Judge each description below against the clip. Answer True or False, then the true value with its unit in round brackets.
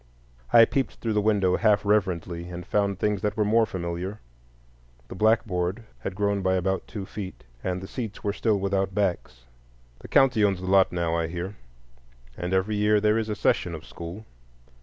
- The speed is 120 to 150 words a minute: False (185 wpm)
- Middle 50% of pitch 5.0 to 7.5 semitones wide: False (2.8 semitones)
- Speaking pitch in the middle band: False (100 Hz)